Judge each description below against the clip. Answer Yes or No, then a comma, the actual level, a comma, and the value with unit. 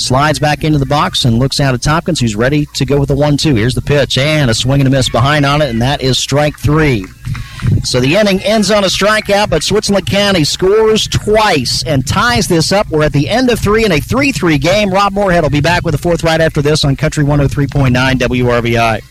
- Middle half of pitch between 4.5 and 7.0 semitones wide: Yes, average, 4.9 semitones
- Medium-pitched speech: Yes, medium, 145 Hz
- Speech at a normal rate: No, fast, 235 wpm